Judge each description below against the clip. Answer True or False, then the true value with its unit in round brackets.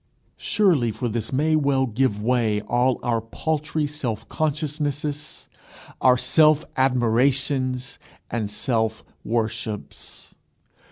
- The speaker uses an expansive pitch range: False (4.4 semitones)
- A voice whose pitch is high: False (130 Hz)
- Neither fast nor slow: False (100 wpm)